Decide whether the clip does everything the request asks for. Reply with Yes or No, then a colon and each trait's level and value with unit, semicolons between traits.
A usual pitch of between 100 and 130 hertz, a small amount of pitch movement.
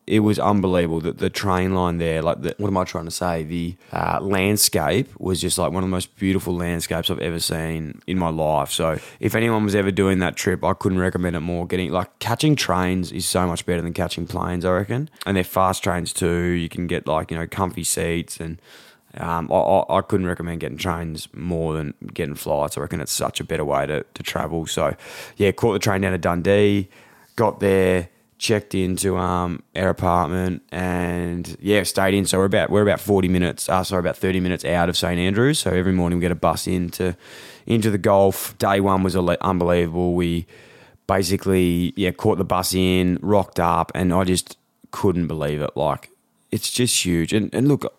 No: very low, 90 Hz; narrow, 2.0 semitones